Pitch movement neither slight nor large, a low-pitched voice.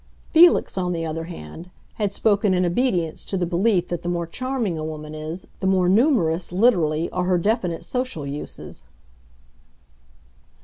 No: average, 3.8 semitones; medium, 180 Hz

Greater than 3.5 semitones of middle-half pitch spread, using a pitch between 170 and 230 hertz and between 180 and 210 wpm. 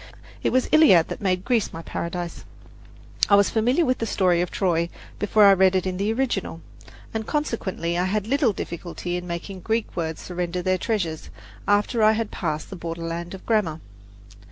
Yes: average, 4.2 semitones; high, 190 Hz; average, 190 wpm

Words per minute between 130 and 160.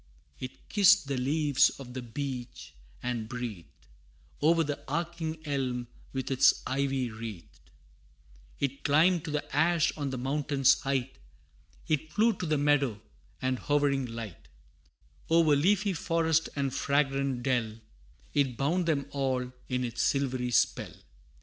Yes: slow, 135 wpm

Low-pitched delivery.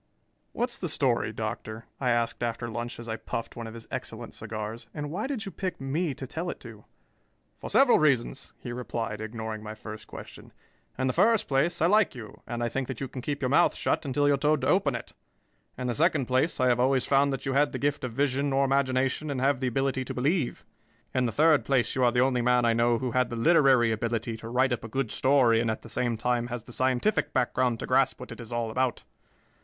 Yes: low, 125 Hz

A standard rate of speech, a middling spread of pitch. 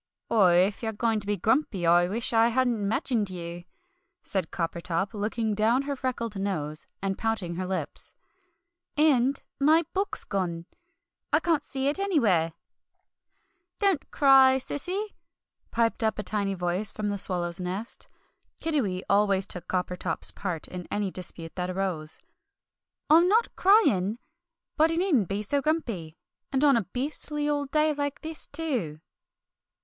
No: average, 150 wpm; wide, 7.5 semitones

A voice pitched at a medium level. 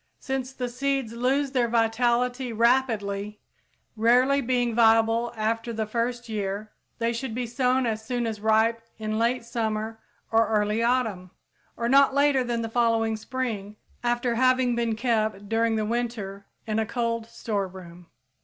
No: high, 230 Hz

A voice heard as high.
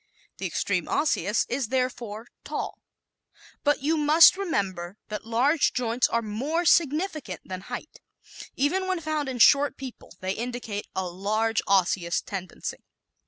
Yes: high, 245 Hz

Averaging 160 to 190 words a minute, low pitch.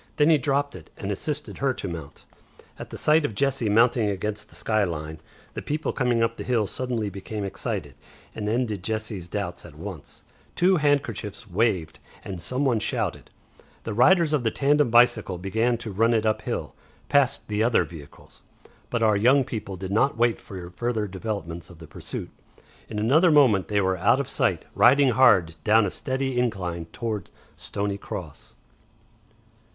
Yes: average, 175 wpm; low, 110 Hz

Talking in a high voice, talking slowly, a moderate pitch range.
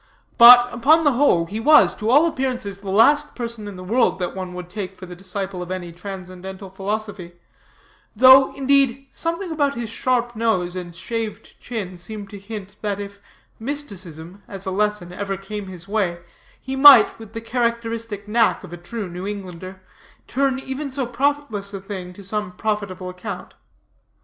No: high, 210 Hz; average, 175 wpm; average, 4.5 semitones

